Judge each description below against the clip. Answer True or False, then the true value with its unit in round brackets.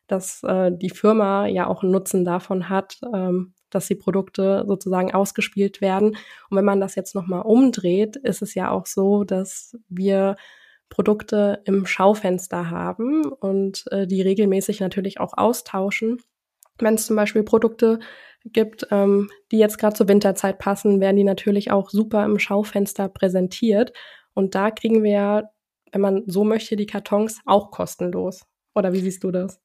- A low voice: False (200 Hz)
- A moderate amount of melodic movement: False (1.9 semitones)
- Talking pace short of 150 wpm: False (160 wpm)